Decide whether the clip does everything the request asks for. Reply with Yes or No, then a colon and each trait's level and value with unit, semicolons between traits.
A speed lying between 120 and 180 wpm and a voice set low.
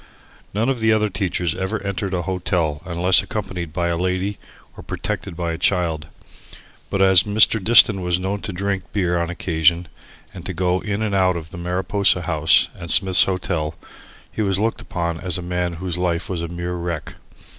No: average, 190 wpm; very low, 90 Hz